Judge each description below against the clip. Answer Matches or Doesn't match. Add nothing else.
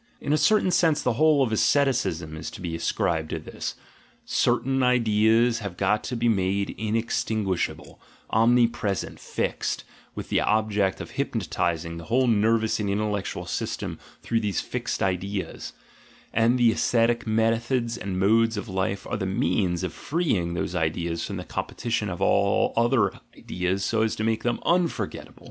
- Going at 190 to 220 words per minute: Doesn't match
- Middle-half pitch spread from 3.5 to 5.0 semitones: Matches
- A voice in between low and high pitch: Doesn't match